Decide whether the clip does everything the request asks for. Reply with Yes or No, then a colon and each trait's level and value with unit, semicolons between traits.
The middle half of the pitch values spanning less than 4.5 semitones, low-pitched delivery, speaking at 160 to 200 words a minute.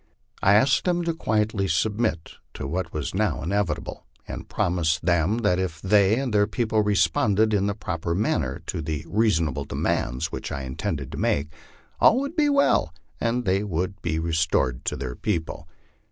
No: average, 5.1 semitones; very low, 95 Hz; average, 175 wpm